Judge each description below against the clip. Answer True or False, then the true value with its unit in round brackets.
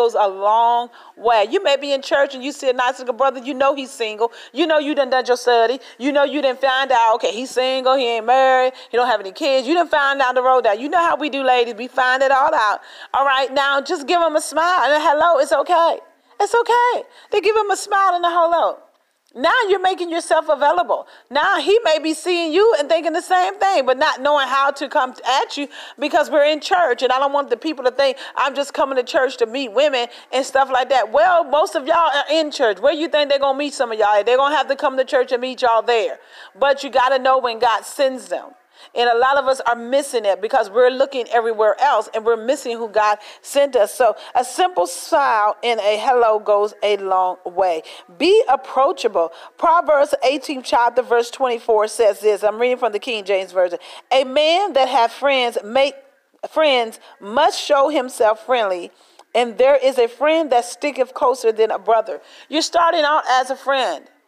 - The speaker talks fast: True (230 wpm)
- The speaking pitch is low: False (270 Hz)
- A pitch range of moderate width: True (4.2 semitones)